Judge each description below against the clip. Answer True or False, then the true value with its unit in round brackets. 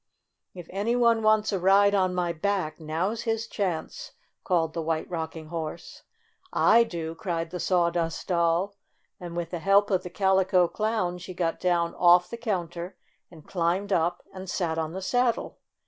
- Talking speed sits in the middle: True (180 wpm)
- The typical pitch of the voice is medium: True (180 Hz)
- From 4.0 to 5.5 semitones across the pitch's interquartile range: False (3.0 semitones)